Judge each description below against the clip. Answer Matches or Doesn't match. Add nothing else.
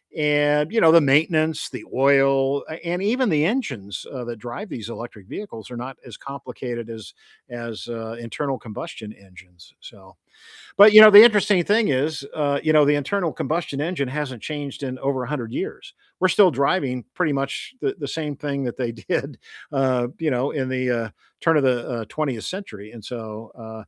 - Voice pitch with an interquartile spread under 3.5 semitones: Doesn't match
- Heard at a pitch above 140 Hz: Doesn't match